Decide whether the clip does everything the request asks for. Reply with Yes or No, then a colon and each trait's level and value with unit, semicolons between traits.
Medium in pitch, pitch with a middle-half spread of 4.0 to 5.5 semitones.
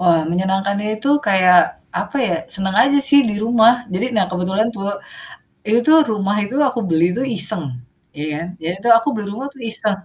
No: high, 210 Hz; average, 4.3 semitones